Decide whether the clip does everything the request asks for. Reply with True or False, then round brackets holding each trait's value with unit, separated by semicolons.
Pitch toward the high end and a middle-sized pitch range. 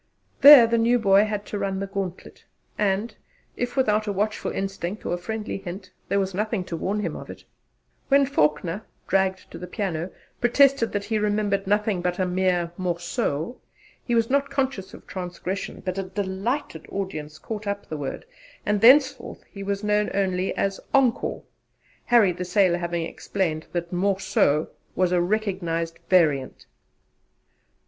True (195 Hz; 3.1 semitones)